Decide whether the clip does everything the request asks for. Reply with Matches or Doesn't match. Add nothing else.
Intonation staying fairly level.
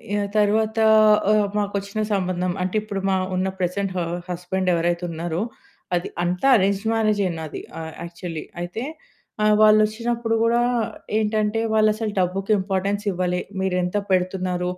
Doesn't match